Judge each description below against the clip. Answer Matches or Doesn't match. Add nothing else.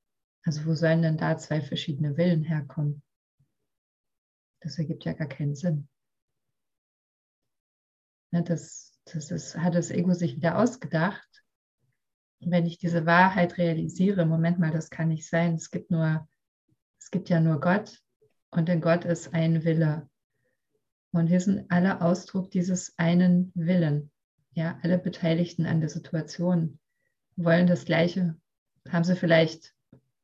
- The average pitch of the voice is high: Doesn't match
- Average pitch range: Doesn't match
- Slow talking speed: Doesn't match